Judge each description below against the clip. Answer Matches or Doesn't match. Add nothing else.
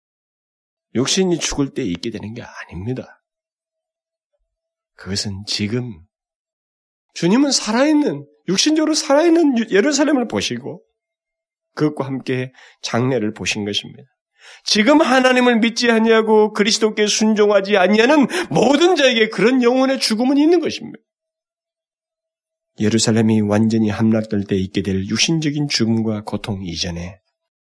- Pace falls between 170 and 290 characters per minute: Matches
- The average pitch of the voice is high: Matches